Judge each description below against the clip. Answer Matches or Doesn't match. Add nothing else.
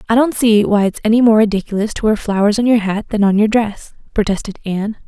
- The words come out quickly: Matches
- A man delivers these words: Doesn't match